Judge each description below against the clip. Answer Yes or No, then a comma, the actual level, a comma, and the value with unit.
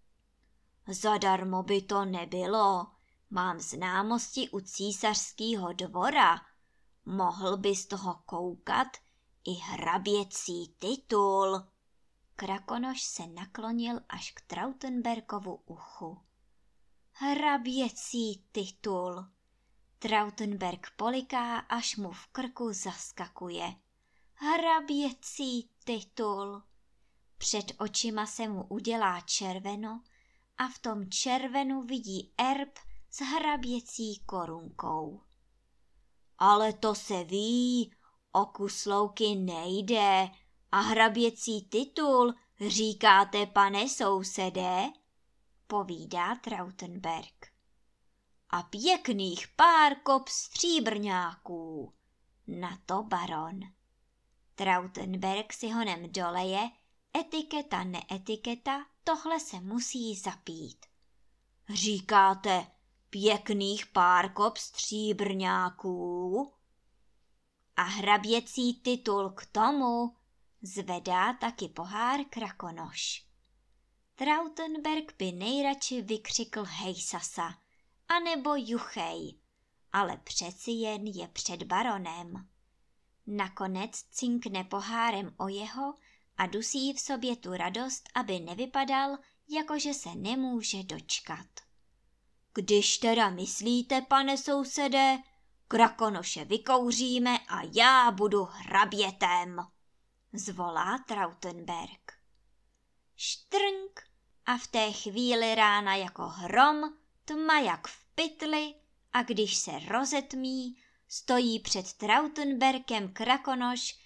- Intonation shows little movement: No, average, 4.7 semitones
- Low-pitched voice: No, high, 215 Hz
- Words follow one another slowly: Yes, slow, 85 wpm